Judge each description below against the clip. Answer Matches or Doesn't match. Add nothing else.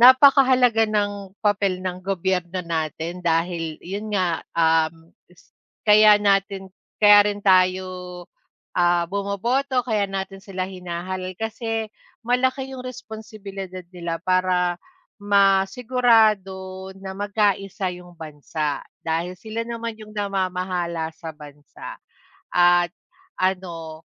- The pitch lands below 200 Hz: Matches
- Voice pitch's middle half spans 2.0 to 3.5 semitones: Matches